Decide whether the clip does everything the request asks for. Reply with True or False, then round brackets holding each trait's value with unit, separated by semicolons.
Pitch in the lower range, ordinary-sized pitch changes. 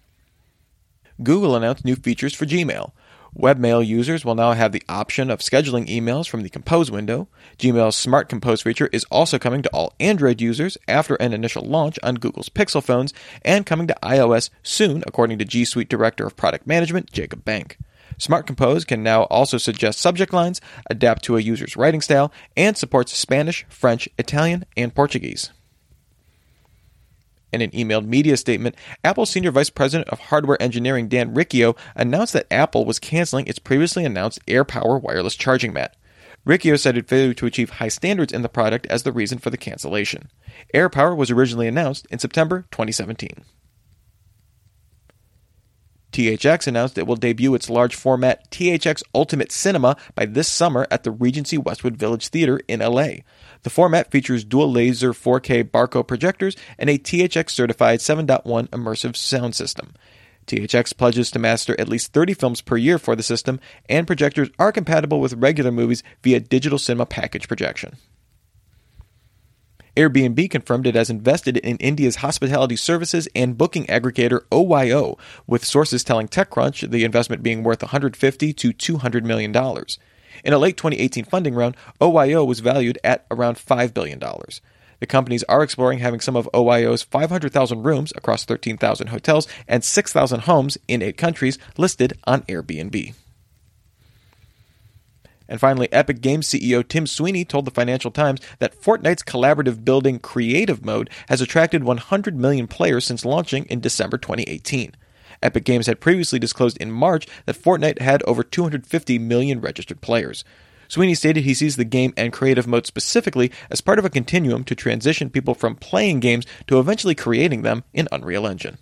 True (125 Hz; 4.2 semitones)